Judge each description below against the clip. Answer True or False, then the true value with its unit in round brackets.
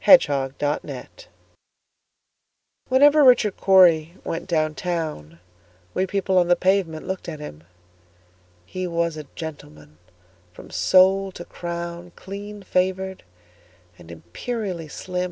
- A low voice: False (170 Hz)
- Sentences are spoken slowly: True (100 wpm)